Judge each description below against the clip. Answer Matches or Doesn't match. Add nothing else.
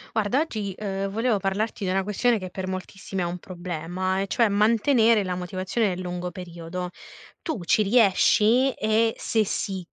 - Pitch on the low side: Doesn't match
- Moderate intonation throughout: Matches